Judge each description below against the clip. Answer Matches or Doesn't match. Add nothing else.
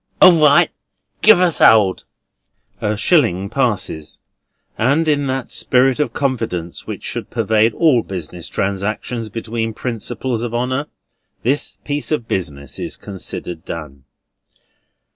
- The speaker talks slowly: Matches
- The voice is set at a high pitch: Doesn't match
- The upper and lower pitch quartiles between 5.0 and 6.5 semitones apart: Matches